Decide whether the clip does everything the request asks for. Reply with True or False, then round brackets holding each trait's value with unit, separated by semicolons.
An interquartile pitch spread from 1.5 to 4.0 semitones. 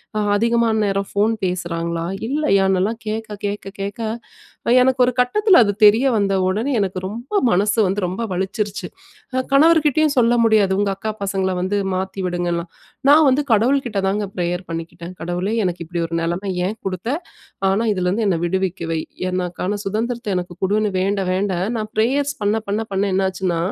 True (3.6 semitones)